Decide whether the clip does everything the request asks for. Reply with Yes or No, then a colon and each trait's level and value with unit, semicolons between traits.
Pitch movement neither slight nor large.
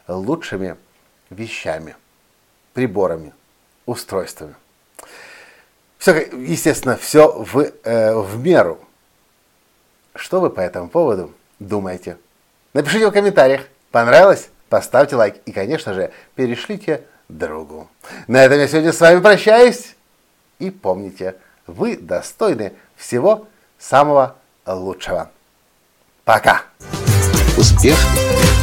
No: wide, 8.8 semitones